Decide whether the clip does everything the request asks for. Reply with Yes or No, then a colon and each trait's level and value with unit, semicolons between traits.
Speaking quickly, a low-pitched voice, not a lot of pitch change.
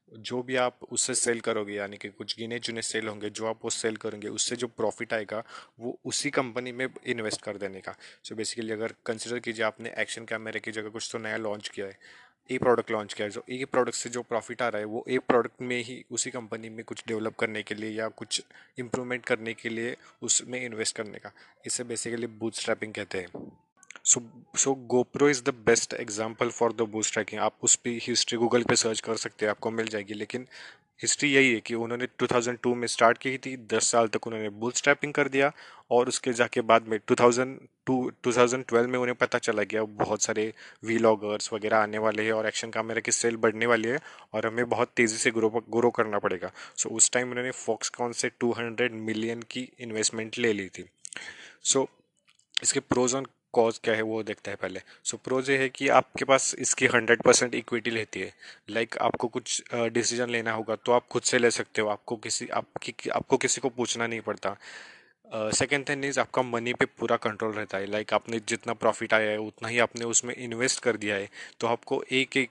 Yes: fast, 215 wpm; low, 115 Hz; narrow, 2.0 semitones